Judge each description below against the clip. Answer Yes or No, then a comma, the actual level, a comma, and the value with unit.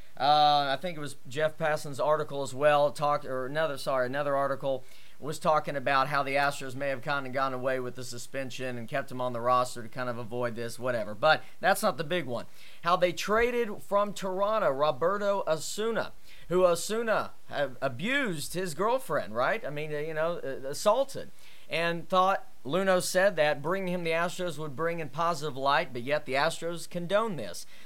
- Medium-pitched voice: Yes, medium, 150 Hz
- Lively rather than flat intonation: No, average, 4.7 semitones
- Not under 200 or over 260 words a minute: No, average, 185 wpm